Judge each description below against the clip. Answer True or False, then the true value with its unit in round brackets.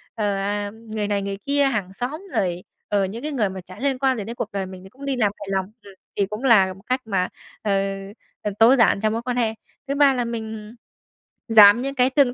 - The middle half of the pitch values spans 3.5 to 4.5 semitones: True (4.1 semitones)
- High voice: True (220 Hz)